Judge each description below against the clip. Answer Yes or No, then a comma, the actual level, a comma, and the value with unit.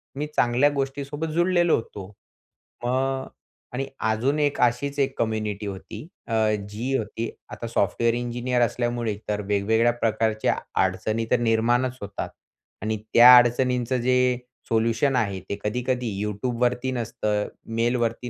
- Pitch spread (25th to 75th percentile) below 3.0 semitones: Yes, narrow, 2.5 semitones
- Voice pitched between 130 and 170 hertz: No, low, 120 Hz